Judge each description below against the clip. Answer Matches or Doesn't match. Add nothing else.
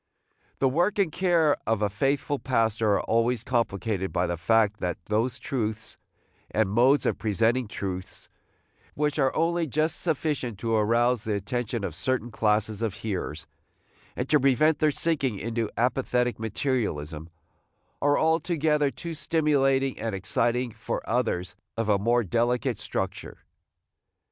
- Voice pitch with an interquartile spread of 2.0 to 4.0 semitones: Doesn't match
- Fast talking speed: Doesn't match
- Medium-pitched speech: Doesn't match